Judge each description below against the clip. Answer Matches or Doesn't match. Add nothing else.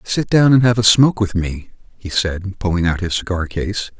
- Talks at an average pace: Doesn't match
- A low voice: Matches